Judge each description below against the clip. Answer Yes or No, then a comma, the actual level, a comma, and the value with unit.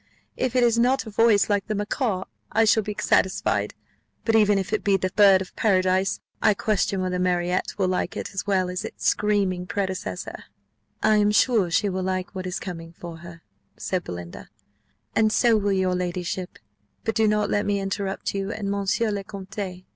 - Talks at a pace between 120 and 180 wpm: No, average, 190 wpm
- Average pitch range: No, narrow, 2.3 semitones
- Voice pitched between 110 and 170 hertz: No, high, 195 Hz